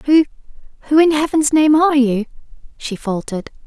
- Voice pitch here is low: No, very high, 280 Hz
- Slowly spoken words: Yes, slow, 130 wpm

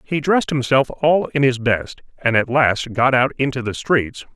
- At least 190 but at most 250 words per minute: Yes, fast, 205 wpm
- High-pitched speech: No, low, 130 Hz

